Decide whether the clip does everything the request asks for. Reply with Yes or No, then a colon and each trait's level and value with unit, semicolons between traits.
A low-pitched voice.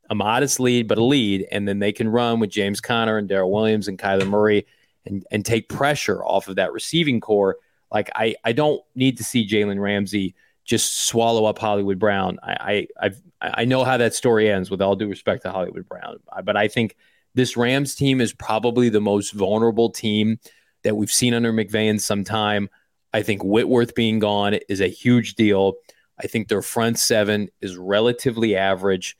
Yes: low, 110 Hz